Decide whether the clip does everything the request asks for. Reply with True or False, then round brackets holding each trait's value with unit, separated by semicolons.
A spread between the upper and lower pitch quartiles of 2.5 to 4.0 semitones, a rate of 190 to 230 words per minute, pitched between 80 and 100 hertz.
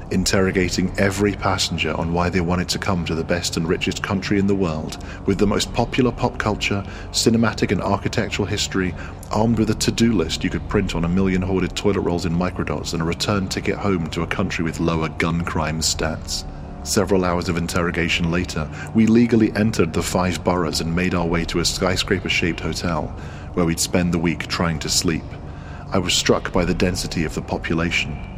True (3.1 semitones; 200 wpm; 90 Hz)